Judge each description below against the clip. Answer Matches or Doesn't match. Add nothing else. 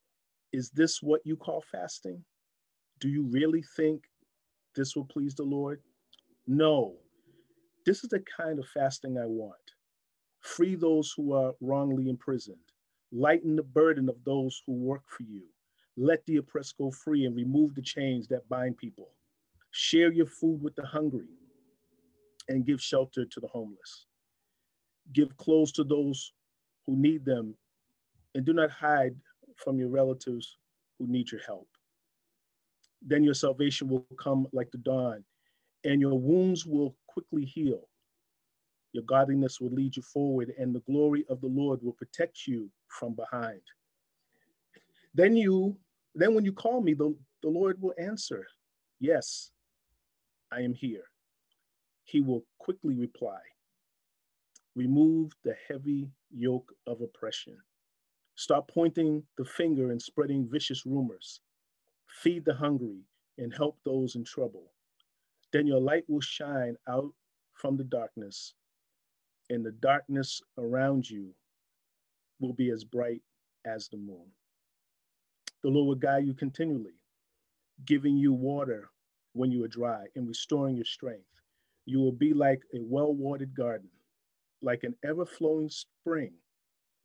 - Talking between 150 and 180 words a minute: Doesn't match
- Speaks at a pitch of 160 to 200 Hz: Doesn't match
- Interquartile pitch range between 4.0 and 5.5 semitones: Doesn't match